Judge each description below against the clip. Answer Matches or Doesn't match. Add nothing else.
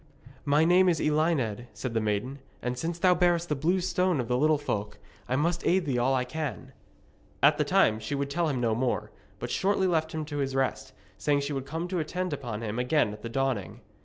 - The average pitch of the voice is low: Doesn't match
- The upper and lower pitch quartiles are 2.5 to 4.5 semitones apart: Doesn't match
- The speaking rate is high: Matches